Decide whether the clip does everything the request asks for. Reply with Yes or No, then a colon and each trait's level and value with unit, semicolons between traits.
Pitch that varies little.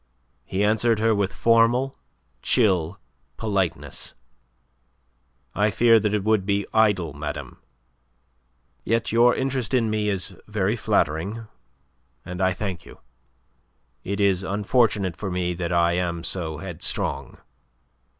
No: average, 3.8 semitones